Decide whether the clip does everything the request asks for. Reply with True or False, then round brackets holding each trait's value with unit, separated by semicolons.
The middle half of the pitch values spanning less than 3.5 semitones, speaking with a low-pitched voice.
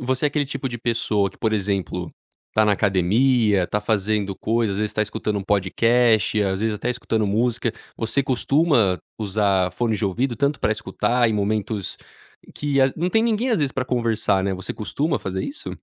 False (3.9 semitones; 110 Hz)